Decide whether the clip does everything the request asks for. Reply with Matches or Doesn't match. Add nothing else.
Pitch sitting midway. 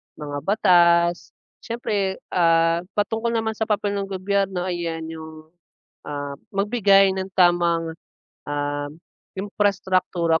Matches